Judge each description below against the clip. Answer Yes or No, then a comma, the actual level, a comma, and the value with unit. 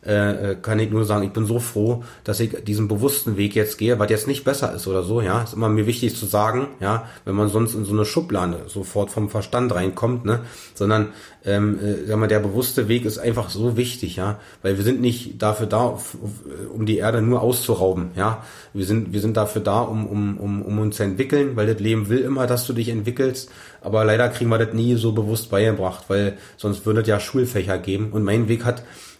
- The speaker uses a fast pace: Yes, fast, 225 wpm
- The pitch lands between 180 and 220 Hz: No, low, 110 Hz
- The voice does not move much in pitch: Yes, narrow, 2.3 semitones